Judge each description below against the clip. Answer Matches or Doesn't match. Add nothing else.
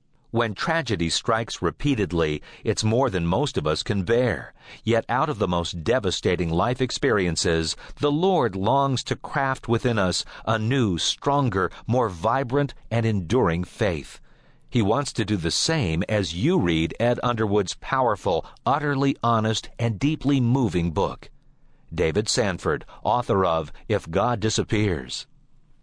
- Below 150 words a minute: Matches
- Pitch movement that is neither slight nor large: Doesn't match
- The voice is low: Matches